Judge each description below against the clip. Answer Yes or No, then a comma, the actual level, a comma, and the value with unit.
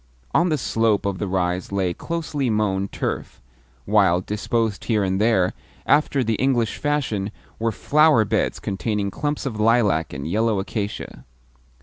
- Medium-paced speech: Yes, average, 145 wpm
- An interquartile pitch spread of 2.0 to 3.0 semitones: No, average, 3.8 semitones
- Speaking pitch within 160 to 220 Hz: No, low, 105 Hz